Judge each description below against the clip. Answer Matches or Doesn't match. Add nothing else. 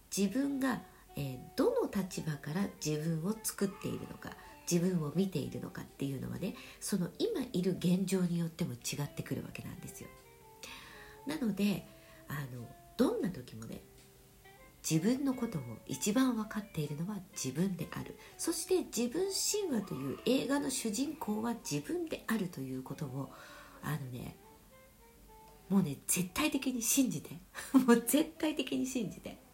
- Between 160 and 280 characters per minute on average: Doesn't match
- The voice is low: Doesn't match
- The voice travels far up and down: Matches